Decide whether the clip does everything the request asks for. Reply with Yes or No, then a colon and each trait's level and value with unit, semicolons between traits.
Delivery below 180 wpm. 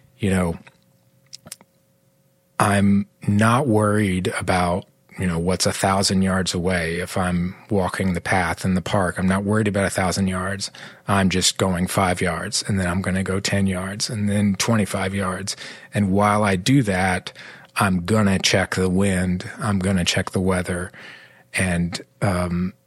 Yes: average, 170 wpm